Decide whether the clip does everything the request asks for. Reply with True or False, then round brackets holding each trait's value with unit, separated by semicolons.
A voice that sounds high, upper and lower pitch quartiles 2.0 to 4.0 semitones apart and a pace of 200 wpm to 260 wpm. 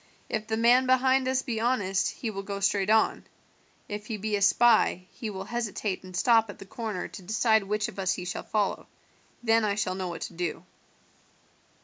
True (210 Hz; 2.8 semitones; 205 wpm)